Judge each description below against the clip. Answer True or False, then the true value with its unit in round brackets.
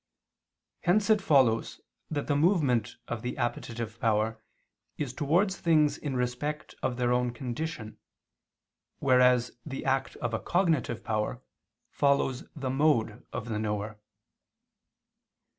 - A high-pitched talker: False (125 Hz)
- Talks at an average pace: False (125 wpm)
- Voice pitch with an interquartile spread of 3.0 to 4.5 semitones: True (4.2 semitones)